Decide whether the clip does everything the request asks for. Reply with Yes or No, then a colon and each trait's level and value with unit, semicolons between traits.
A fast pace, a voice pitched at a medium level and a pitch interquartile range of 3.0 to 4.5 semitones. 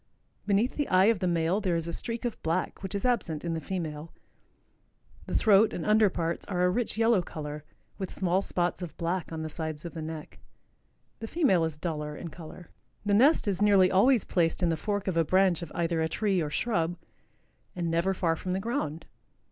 Yes: fast, 210 wpm; medium, 180 Hz; average, 3.7 semitones